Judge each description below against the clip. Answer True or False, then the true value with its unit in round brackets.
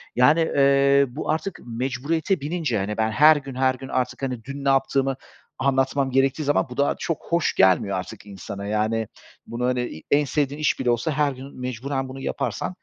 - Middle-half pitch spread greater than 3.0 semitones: False (2.7 semitones)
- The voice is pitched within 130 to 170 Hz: True (135 Hz)